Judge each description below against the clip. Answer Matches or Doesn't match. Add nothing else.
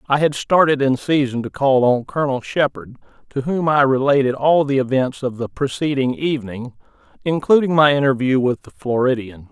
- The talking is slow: Doesn't match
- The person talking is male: Matches